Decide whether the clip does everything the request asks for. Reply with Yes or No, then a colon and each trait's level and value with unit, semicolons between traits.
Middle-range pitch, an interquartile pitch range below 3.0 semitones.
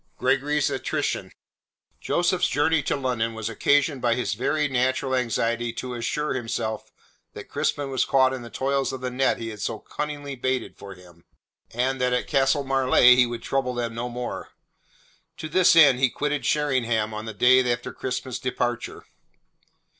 No: low, 130 Hz; narrow, 2.5 semitones